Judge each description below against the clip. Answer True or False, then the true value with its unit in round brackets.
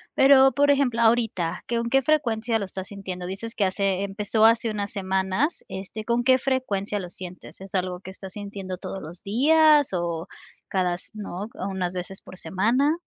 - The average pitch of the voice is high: True (200 Hz)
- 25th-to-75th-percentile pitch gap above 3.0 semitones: True (4.2 semitones)